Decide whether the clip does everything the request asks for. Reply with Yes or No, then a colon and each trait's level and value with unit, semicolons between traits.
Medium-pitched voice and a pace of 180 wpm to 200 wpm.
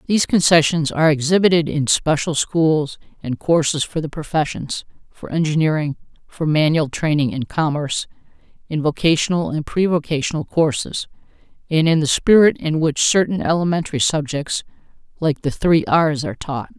No: medium, 155 Hz; average, 140 wpm